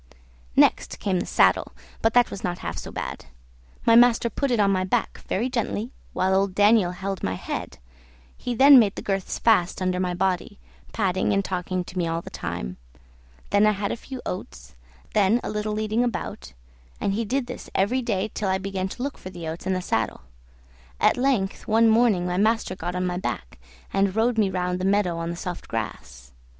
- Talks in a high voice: Yes, high, 195 Hz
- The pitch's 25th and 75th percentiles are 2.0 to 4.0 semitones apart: Yes, average, 3.6 semitones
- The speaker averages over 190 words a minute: Yes, fast, 205 wpm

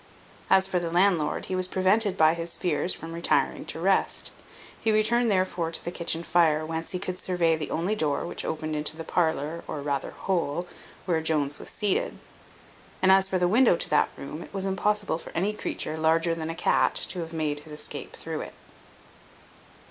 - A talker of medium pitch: Yes, medium, 170 Hz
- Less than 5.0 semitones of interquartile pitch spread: Yes, average, 3.0 semitones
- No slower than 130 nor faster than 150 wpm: No, average, 195 wpm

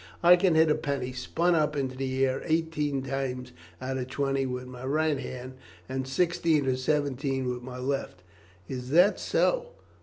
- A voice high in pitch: No, low, 135 Hz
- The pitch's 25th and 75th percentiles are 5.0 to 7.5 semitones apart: No, average, 3.3 semitones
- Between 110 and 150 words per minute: No, average, 175 wpm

